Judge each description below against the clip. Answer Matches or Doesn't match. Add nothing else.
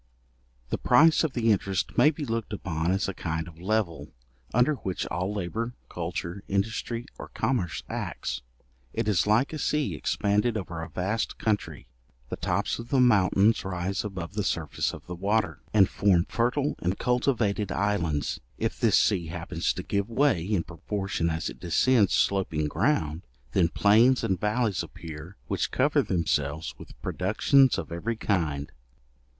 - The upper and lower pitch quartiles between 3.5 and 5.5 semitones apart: Matches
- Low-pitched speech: Matches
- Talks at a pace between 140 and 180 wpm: Matches